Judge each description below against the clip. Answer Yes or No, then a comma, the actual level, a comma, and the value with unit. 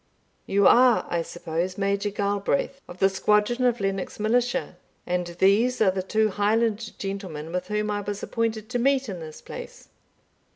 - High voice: Yes, high, 205 Hz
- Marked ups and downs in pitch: No, average, 3.1 semitones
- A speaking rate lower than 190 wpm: Yes, average, 165 wpm